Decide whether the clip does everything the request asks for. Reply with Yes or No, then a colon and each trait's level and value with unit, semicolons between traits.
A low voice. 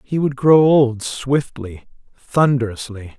Yes: low, 130 Hz